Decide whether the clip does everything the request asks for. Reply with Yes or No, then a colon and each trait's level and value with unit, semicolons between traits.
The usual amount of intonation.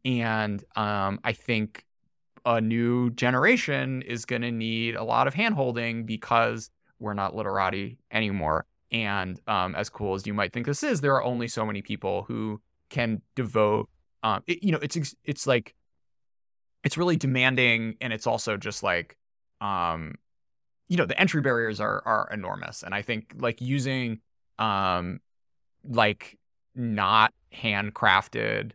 Yes: average, 3.8 semitones